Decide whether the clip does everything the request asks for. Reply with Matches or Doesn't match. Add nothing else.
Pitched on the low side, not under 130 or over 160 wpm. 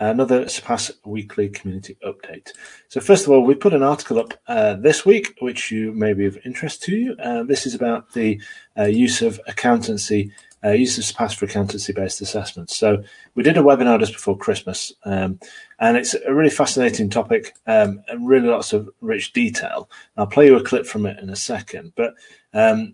Doesn't match